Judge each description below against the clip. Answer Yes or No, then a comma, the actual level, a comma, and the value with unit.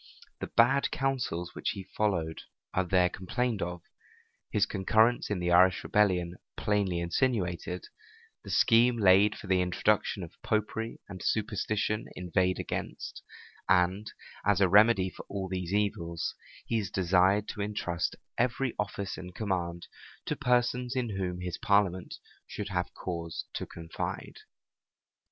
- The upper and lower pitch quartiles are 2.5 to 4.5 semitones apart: Yes, average, 3.2 semitones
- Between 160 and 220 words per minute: No, slow, 135 wpm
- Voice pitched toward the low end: Yes, very low, 95 Hz